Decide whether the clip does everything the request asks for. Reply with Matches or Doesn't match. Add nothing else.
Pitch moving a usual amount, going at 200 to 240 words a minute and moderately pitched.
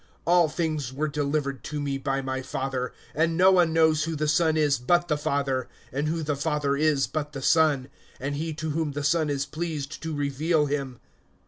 Doesn't match